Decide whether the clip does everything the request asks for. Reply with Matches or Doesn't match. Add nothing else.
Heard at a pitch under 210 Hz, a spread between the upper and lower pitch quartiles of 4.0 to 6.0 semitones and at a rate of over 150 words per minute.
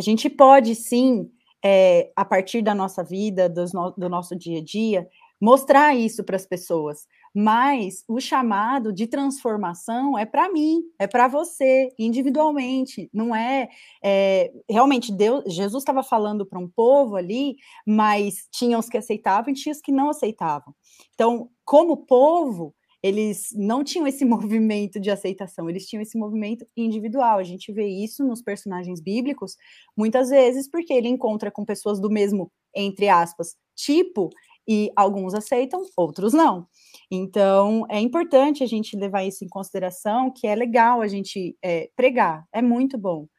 Doesn't match